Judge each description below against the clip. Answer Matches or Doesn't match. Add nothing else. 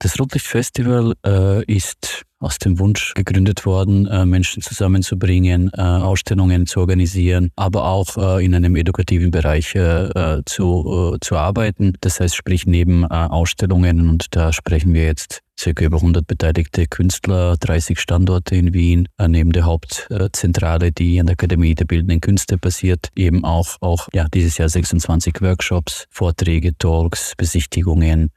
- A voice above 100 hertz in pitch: Doesn't match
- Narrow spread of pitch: Matches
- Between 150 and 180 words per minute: Matches